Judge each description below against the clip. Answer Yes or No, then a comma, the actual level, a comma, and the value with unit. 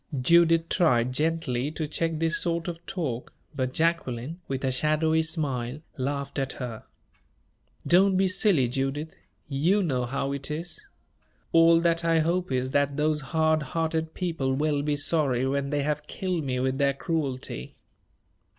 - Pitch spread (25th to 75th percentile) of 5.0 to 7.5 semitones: No, average, 3.6 semitones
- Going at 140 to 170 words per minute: Yes, average, 155 wpm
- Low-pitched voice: No, medium, 150 Hz